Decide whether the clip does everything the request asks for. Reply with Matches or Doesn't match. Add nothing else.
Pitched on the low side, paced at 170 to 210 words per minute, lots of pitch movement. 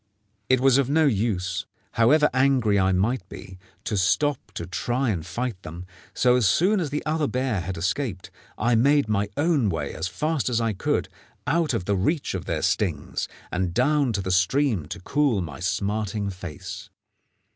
Matches